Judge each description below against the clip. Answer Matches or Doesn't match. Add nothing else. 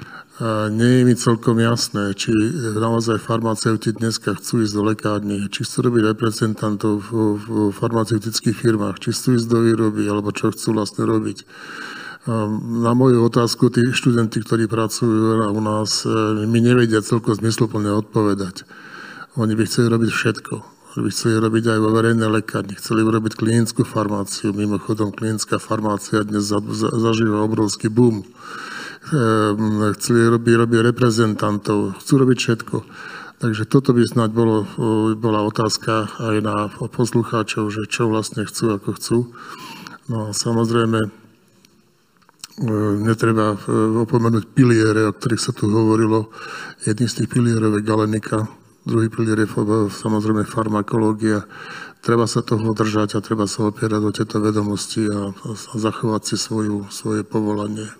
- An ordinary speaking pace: Matches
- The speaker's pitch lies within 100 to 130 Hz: Matches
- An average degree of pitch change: Doesn't match